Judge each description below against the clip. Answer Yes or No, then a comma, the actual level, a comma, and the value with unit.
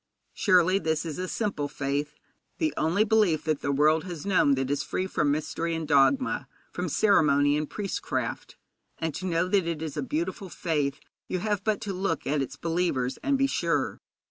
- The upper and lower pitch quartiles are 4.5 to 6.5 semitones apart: Yes, average, 4.8 semitones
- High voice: No, medium, 165 Hz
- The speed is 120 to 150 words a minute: No, average, 190 wpm